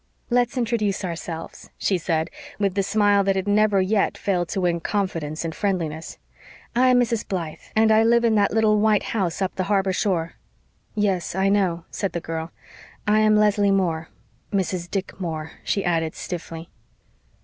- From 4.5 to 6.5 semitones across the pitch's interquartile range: No, average, 3.6 semitones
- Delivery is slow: No, average, 170 wpm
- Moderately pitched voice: No, high, 195 Hz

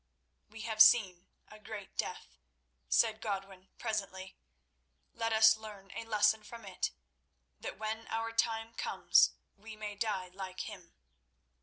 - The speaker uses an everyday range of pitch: No, narrow, 2.3 semitones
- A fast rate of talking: No, slow, 135 wpm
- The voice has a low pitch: No, high, 215 Hz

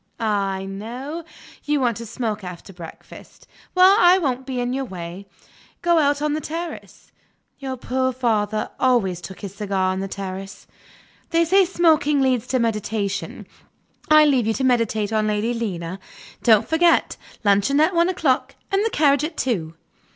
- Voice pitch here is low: No, high, 245 Hz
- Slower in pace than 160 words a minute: No, average, 165 wpm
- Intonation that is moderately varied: No, wide, 6.8 semitones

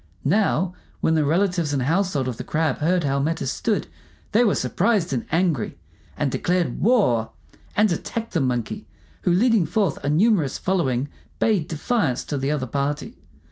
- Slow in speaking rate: No, average, 165 wpm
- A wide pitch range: Yes, wide, 6.0 semitones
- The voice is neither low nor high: Yes, medium, 160 Hz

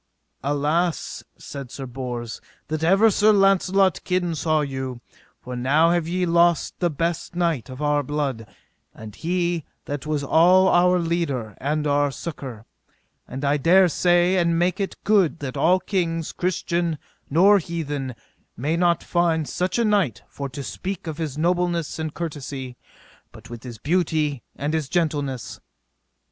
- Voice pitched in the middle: Yes, medium, 160 Hz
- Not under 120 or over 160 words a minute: Yes, average, 150 wpm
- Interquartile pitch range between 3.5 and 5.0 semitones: Yes, average, 3.9 semitones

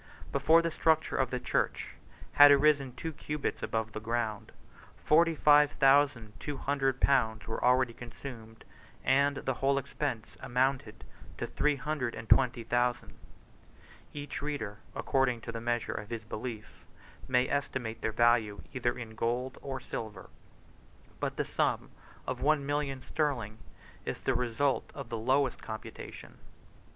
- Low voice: Yes, low, 130 Hz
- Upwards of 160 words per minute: No, average, 145 wpm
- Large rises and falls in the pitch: No, average, 3.6 semitones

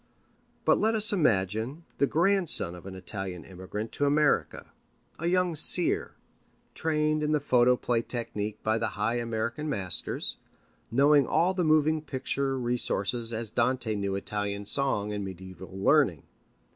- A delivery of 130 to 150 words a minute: Yes, average, 140 wpm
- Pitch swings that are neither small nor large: No, wide, 6.8 semitones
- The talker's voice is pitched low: Yes, low, 120 Hz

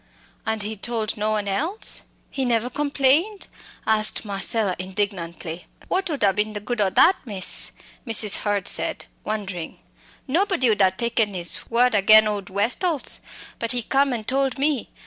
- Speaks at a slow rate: No, average, 160 wpm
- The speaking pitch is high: Yes, high, 220 Hz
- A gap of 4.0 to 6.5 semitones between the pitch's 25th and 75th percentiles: Yes, average, 4.5 semitones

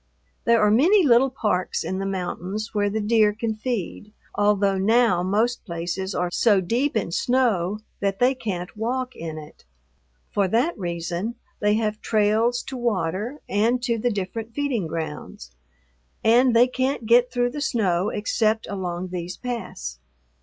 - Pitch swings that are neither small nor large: Yes, average, 4.4 semitones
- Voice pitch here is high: Yes, high, 215 Hz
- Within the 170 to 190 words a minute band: No, average, 155 wpm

